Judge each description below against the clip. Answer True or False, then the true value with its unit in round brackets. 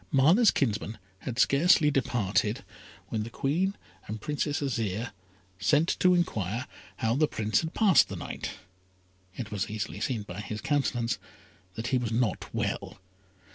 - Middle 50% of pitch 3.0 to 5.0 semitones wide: False (5.4 semitones)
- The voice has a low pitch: True (120 Hz)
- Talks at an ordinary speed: True (145 wpm)